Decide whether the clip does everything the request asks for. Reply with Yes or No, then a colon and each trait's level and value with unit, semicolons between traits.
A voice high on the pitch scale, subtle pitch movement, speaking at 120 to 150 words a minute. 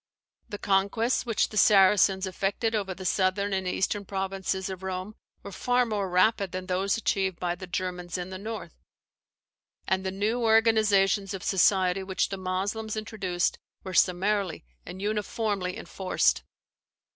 Yes: high, 195 Hz; narrow, 2.0 semitones; average, 145 wpm